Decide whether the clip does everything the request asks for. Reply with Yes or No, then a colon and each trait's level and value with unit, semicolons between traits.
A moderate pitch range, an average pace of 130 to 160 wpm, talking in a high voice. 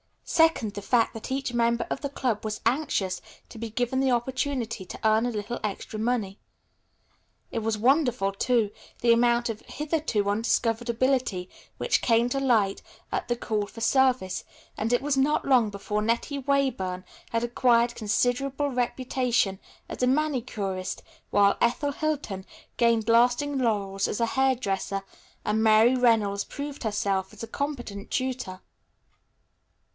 Yes: average, 3.7 semitones; average, 150 wpm; high, 235 Hz